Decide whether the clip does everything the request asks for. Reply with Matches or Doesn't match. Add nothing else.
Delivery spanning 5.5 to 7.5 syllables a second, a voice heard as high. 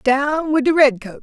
Doesn't match